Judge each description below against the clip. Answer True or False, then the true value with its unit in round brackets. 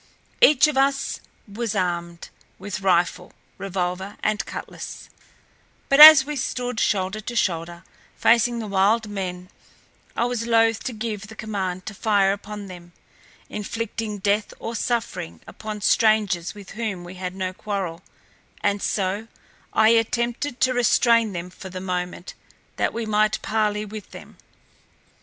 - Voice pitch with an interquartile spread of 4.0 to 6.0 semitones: False (3.5 semitones)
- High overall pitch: True (210 Hz)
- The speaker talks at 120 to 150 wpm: True (145 wpm)